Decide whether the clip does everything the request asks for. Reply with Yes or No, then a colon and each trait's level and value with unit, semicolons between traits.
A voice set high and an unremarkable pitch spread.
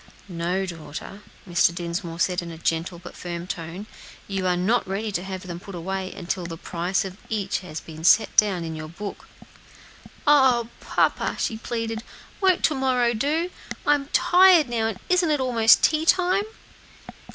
No: high, 195 Hz; wide, 6.2 semitones